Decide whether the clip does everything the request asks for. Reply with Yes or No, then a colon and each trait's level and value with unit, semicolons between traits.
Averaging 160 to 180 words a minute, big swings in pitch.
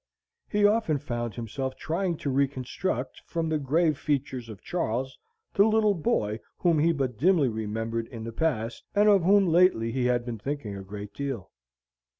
Yes: average, 170 wpm; wide, 6.5 semitones